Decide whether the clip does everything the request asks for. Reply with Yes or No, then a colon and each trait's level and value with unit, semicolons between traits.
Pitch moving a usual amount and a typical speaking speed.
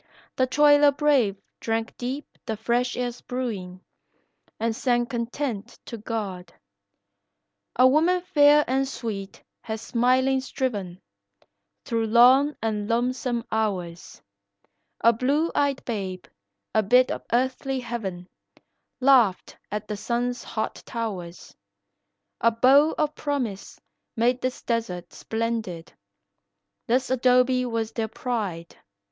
No: average, 3.0 semitones; slow, 115 wpm